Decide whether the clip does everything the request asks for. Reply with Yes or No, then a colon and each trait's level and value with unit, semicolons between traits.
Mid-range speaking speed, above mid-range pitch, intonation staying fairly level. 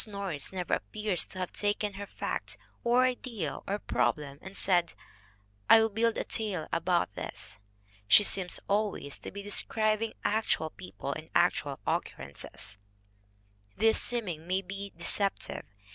No: average, 145 wpm; high, 195 Hz; average, 4.0 semitones